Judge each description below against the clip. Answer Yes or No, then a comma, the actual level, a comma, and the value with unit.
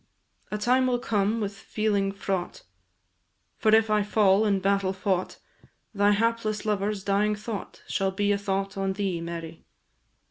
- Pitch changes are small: Yes, narrow, 1.6 semitones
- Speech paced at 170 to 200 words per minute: No, average, 150 wpm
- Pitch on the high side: Yes, high, 200 Hz